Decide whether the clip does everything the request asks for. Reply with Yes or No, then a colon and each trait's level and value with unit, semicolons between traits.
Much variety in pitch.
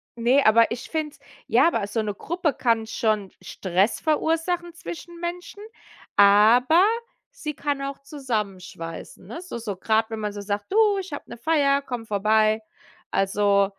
Yes: wide, 7.3 semitones